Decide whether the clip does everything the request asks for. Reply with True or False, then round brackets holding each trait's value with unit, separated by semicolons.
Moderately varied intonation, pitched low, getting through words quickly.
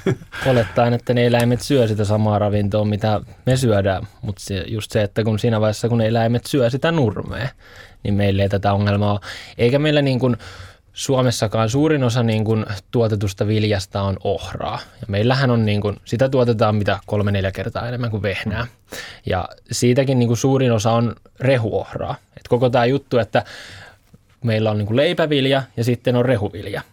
True (3.2 semitones; 110 Hz; 170 wpm)